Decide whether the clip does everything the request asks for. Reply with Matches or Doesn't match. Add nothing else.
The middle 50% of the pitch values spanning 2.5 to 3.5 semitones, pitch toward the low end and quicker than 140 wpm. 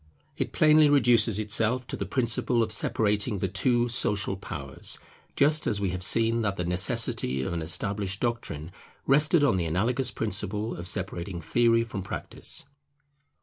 Doesn't match